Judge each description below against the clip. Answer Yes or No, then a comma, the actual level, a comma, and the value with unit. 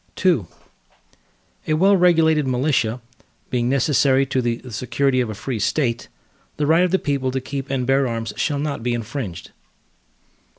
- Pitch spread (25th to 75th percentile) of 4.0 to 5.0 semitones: No, average, 3.6 semitones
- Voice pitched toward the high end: No, low, 135 Hz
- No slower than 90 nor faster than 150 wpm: No, average, 160 wpm